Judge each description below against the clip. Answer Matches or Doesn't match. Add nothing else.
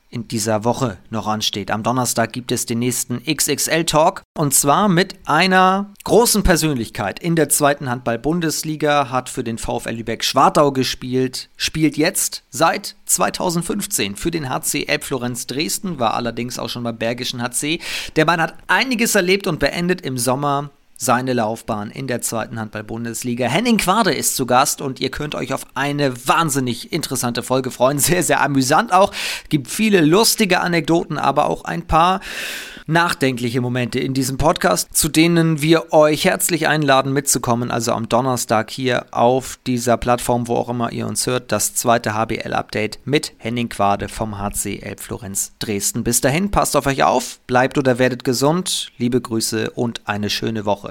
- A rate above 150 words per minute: Matches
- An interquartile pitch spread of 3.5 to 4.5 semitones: Doesn't match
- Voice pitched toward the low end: Matches